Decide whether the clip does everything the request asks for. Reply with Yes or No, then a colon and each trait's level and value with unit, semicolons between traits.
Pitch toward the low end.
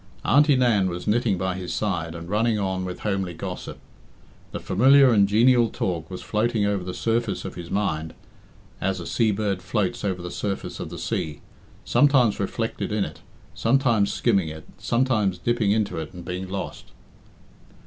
Yes: low, 100 Hz